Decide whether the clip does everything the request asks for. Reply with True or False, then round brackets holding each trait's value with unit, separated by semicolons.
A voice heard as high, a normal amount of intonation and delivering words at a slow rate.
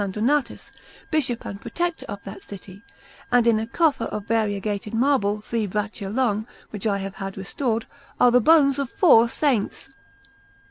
False (225 Hz; 4.1 semitones; 155 wpm)